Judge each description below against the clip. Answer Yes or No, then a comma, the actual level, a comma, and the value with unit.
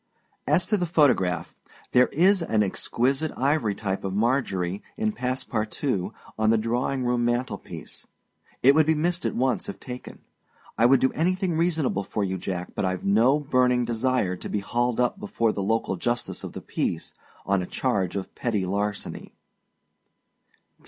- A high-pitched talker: No, low, 120 Hz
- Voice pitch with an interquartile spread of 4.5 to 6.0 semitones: Yes, average, 5.3 semitones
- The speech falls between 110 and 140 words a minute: No, average, 170 wpm